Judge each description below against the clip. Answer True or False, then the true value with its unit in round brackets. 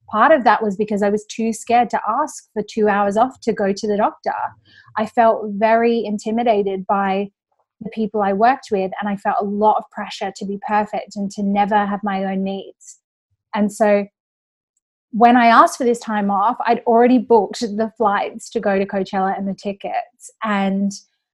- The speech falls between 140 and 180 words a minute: False (195 wpm)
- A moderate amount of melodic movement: False (2.3 semitones)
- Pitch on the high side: True (210 Hz)